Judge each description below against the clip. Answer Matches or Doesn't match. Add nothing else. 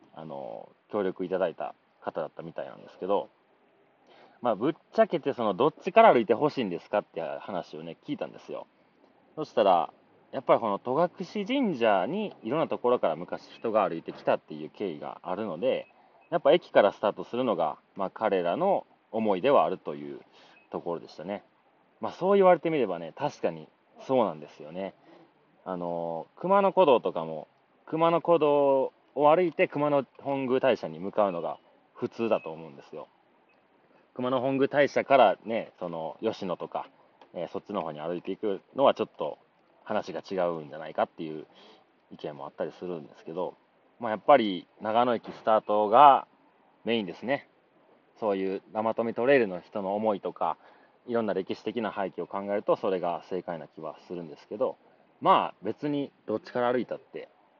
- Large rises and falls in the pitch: Matches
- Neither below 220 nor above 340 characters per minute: Doesn't match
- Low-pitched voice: Matches